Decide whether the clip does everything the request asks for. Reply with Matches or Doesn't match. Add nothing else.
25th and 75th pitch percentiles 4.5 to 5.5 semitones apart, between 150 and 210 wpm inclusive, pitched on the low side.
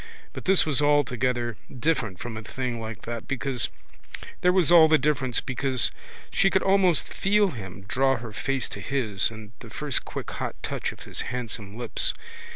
Matches